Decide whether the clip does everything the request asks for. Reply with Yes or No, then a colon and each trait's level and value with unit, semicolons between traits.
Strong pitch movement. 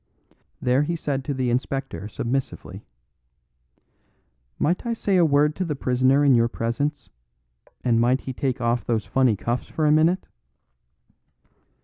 No: average, 3.5 semitones